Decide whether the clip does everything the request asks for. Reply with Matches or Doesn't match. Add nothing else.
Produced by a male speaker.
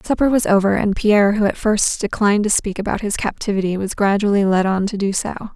Doesn't match